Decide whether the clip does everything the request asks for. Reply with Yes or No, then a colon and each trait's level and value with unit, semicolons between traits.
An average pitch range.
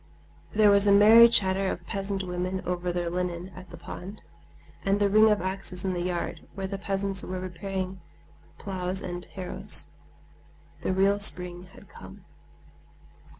No: narrow, 1.7 semitones